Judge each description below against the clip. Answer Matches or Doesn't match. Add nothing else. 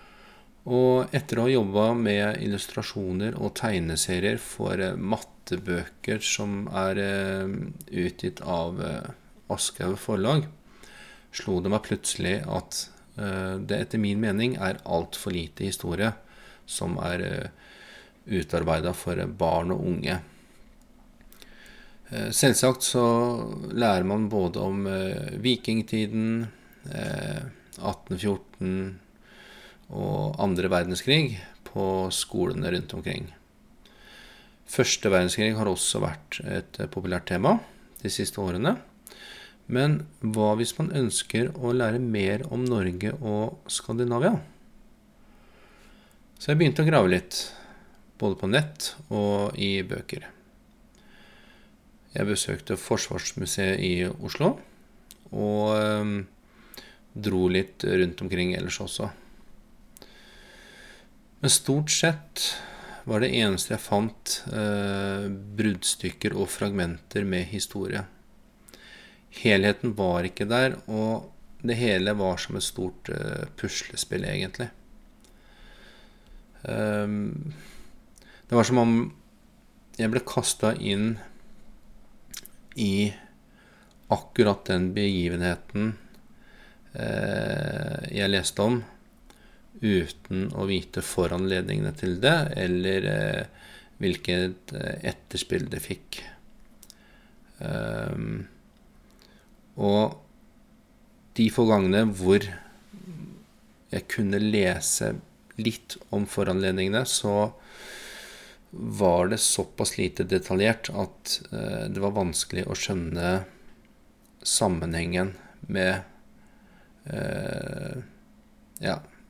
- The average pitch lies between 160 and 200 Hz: Doesn't match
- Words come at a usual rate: Doesn't match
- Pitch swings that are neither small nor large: Matches